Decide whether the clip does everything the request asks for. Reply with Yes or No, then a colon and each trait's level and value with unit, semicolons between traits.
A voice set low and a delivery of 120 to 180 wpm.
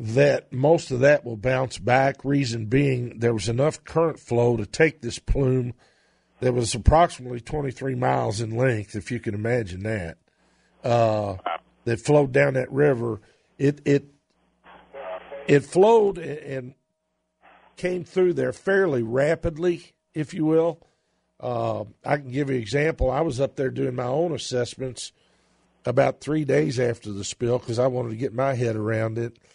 Yes: low, 130 Hz; average, 160 wpm